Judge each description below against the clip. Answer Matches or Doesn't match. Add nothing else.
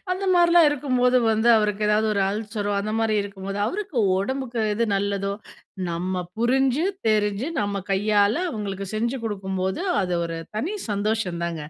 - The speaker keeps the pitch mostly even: Doesn't match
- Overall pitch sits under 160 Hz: Doesn't match